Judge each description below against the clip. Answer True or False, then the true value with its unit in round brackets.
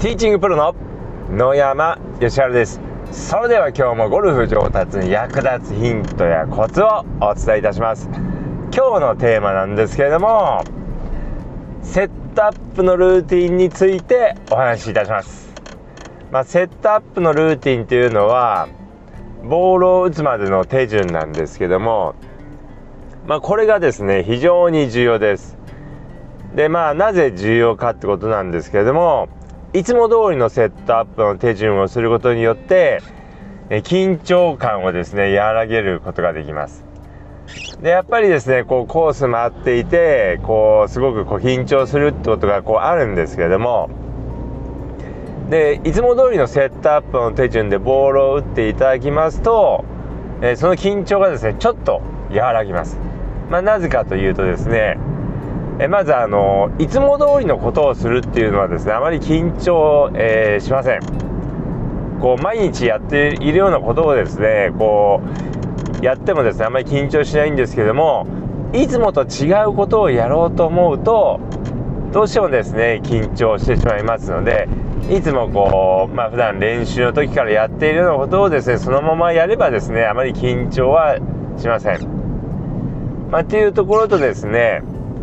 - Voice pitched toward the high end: False (135 Hz)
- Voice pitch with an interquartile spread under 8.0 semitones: False (8.3 semitones)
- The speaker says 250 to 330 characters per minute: True (325 characters per minute)